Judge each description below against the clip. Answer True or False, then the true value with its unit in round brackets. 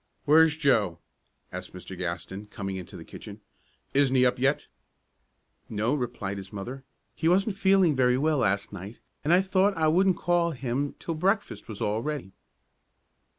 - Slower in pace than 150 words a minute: False (160 wpm)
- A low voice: True (130 Hz)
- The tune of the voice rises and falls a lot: True (8.0 semitones)